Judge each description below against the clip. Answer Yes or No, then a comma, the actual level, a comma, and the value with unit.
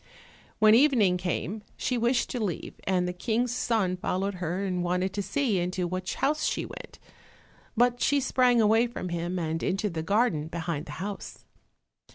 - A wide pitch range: No, average, 4.8 semitones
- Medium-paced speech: Yes, average, 175 wpm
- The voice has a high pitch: Yes, high, 195 Hz